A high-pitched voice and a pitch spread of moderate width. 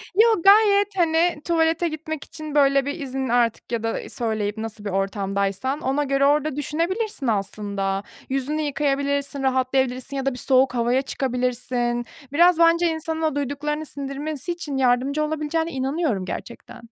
Yes: very high, 275 Hz; average, 4.2 semitones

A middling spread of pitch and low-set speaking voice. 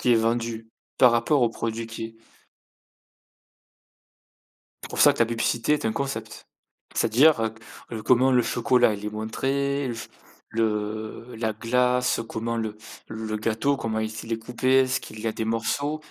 No: narrow, 2.2 semitones; low, 115 Hz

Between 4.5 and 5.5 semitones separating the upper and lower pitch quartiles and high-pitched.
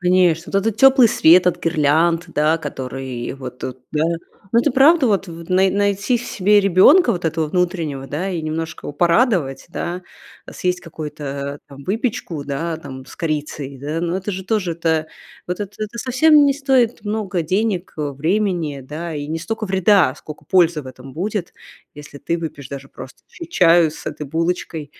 No: average, 4.9 semitones; medium, 170 Hz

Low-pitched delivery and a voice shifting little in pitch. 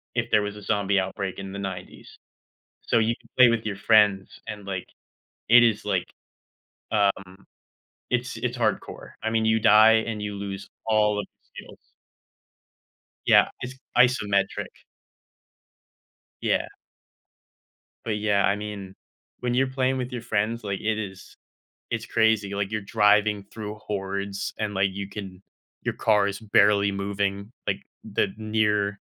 Yes: low, 105 Hz; narrow, 1.9 semitones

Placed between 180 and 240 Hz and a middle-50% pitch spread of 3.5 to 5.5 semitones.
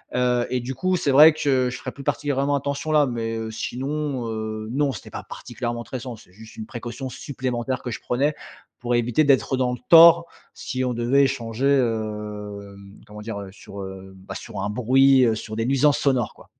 No: low, 125 Hz; average, 3.8 semitones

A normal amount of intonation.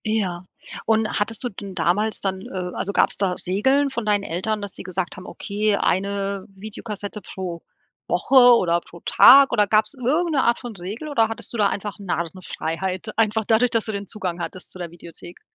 Yes: average, 3.2 semitones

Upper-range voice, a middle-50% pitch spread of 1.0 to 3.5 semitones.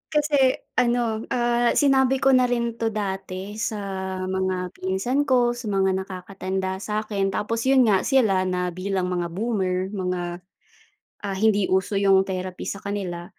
No: high, 195 Hz; average, 4.0 semitones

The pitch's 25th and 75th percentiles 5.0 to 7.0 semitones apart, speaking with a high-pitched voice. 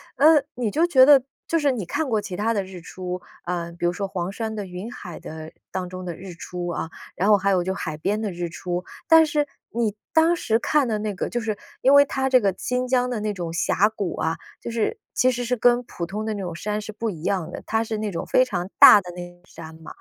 Yes: average, 5.3 semitones; high, 205 Hz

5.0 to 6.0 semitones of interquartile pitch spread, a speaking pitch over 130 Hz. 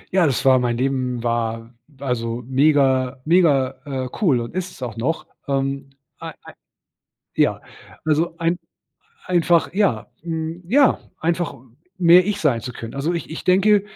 Yes: average, 5.3 semitones; medium, 140 Hz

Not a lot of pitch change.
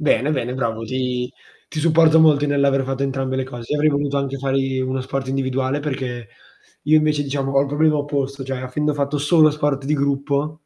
Yes: narrow, 1.8 semitones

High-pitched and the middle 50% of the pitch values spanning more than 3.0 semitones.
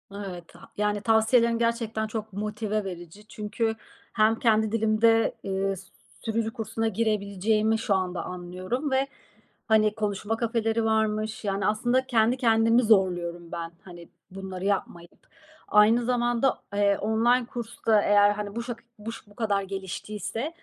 No: high, 215 Hz; narrow, 2.4 semitones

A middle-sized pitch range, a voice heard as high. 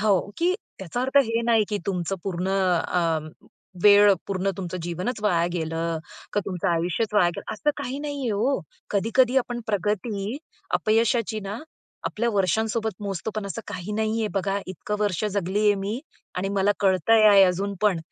Yes: average, 3.1 semitones; high, 205 Hz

